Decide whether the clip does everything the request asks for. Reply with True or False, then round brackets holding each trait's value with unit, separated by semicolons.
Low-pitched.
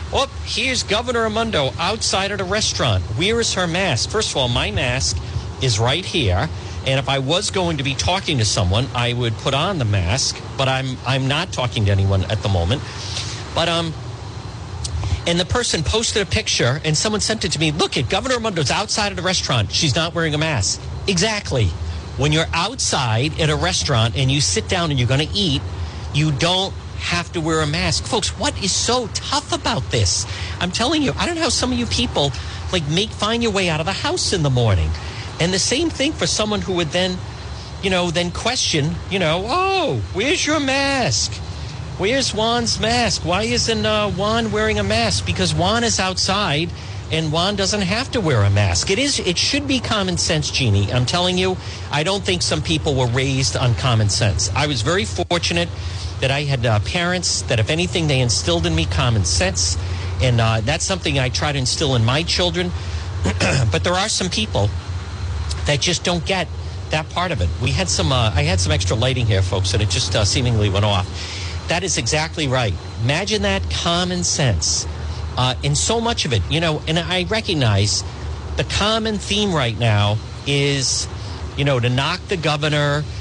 True (120 Hz)